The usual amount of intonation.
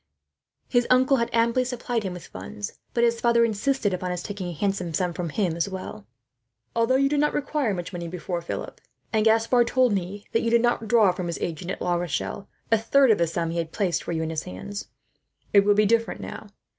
Yes: average, 5.0 semitones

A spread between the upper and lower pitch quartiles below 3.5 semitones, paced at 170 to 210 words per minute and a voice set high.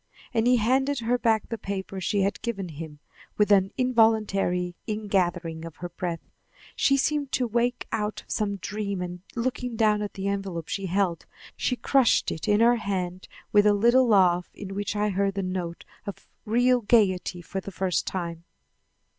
No: average, 3.9 semitones; average, 180 wpm; high, 200 Hz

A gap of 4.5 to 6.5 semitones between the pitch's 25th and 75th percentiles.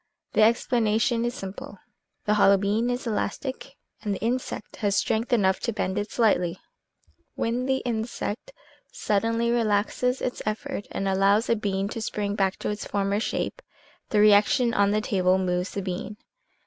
No: average, 2.8 semitones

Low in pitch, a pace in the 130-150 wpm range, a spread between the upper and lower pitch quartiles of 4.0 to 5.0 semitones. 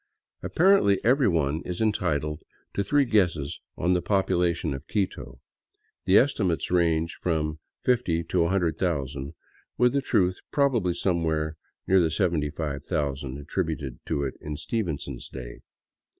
Yes: very low, 85 Hz; average, 140 wpm; average, 4.5 semitones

